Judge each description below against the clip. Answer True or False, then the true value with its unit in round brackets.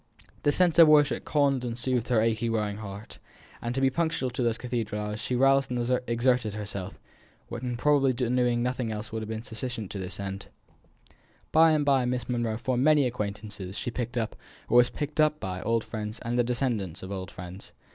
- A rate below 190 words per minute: False (195 wpm)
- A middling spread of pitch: True (3.5 semitones)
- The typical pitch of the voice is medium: False (120 Hz)